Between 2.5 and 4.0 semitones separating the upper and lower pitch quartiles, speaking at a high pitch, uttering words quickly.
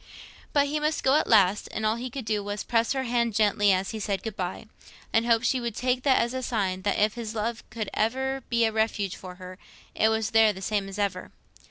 Yes: average, 2.9 semitones; high, 220 Hz; fast, 250 wpm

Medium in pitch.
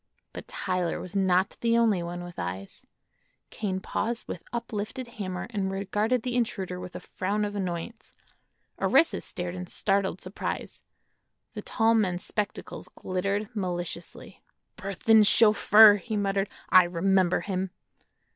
No: high, 195 Hz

